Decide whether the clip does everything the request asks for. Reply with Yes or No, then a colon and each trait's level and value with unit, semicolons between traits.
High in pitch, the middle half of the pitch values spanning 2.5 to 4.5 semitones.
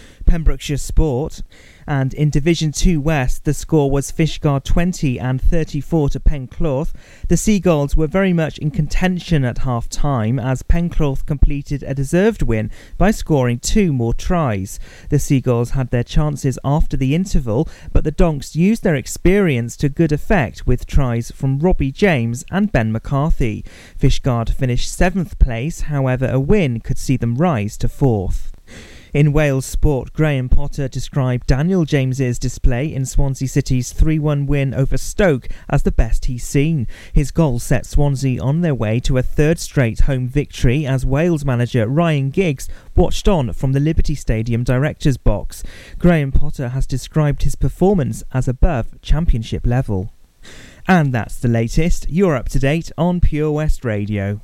No: medium, 140 Hz; average, 4.1 semitones